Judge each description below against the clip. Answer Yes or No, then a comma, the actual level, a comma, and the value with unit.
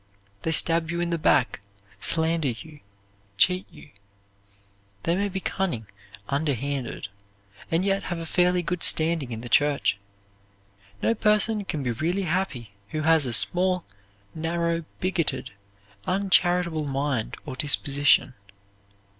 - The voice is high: No, medium, 165 Hz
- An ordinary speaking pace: No, slow, 130 wpm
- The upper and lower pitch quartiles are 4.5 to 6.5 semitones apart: No, average, 4.1 semitones